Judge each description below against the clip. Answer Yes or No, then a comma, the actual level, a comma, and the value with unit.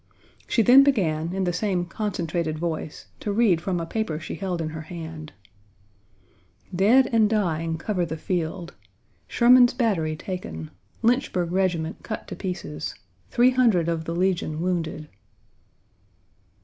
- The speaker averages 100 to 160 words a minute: Yes, slow, 135 wpm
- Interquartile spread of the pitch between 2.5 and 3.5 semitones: No, average, 4.7 semitones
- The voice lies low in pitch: No, medium, 175 Hz